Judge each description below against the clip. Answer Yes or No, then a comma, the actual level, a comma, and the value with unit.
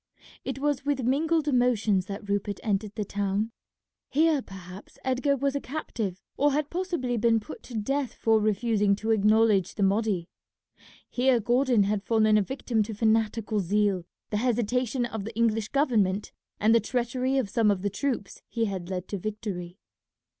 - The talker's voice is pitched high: Yes, high, 220 Hz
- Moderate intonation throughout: Yes, average, 3.9 semitones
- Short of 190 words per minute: Yes, average, 170 wpm